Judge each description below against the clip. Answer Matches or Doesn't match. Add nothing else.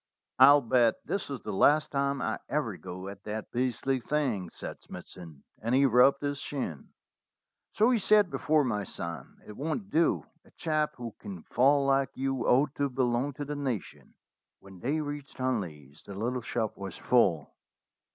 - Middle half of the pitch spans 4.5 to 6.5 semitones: Matches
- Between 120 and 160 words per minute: Doesn't match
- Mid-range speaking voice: Doesn't match